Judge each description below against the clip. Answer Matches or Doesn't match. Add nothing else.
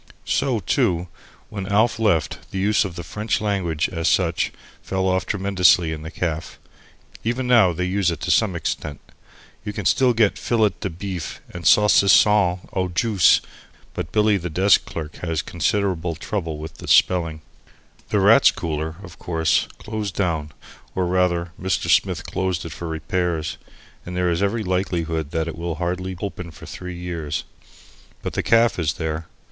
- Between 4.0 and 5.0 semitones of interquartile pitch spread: Doesn't match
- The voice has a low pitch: Matches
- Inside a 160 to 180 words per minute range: Matches